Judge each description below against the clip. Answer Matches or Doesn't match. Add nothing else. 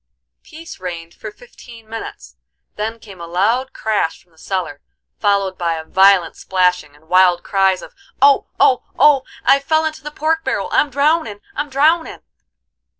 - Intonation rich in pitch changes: Matches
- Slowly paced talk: Doesn't match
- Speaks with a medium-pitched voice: Doesn't match